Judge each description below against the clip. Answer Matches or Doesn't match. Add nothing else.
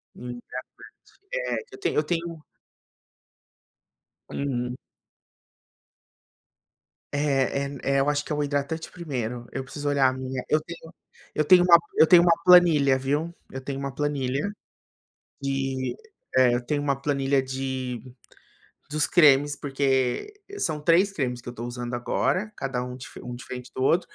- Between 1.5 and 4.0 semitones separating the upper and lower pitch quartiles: Matches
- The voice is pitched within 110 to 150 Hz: Matches